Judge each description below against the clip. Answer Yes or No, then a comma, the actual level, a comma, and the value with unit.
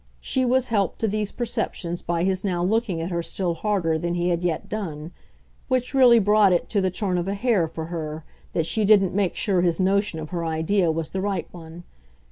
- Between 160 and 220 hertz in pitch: Yes, medium, 185 Hz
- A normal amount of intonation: Yes, average, 3.7 semitones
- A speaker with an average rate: No, fast, 220 wpm